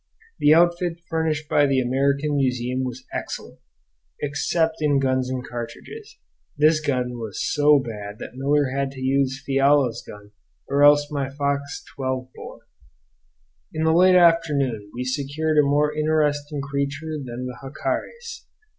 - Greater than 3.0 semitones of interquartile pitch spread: No, narrow, 2.6 semitones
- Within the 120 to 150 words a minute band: Yes, average, 145 wpm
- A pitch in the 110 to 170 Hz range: Yes, medium, 140 Hz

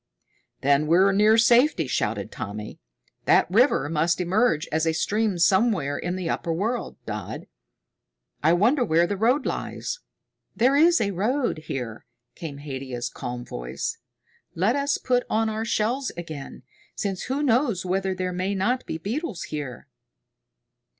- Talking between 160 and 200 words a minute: No, average, 145 wpm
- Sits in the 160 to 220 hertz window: Yes, high, 190 Hz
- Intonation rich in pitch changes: Yes, wide, 7.0 semitones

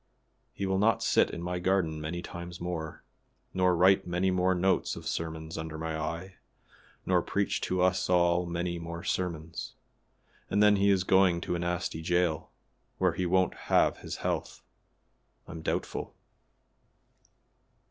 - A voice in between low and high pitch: No, very low, 90 Hz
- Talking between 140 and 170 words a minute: Yes, average, 150 wpm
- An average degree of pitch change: No, narrow, 1.9 semitones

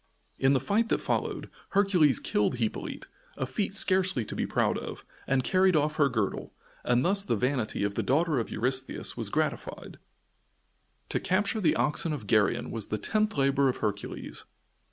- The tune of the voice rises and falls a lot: Yes, wide, 7.7 semitones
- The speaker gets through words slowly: No, average, 175 wpm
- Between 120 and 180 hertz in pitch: Yes, low, 135 Hz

